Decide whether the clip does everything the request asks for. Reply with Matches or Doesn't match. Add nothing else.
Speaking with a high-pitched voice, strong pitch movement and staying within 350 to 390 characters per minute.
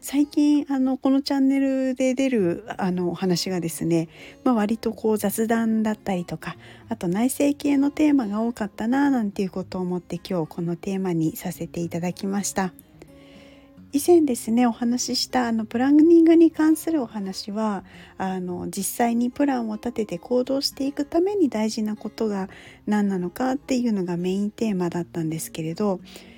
Matches